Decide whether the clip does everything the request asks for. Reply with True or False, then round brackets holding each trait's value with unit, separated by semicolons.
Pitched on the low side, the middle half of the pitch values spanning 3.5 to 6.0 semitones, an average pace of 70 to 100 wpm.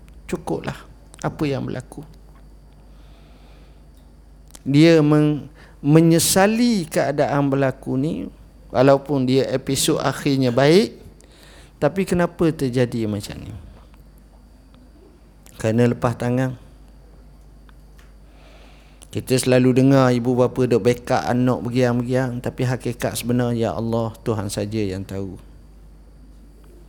True (125 Hz; 5.1 semitones; 90 wpm)